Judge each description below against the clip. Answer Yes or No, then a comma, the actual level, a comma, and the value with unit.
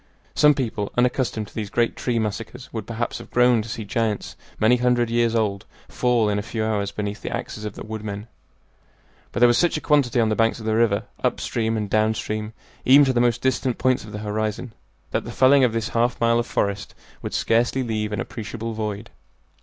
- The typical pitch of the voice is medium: No, low, 115 Hz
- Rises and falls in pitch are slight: Yes, narrow, 2.3 semitones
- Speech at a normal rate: No, fast, 215 wpm